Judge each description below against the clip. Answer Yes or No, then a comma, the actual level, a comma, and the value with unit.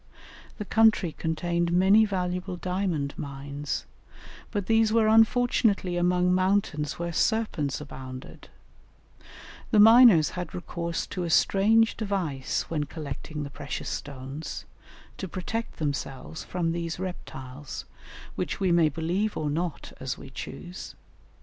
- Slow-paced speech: Yes, slow, 125 wpm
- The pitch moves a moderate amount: Yes, average, 5.0 semitones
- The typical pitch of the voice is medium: Yes, medium, 175 Hz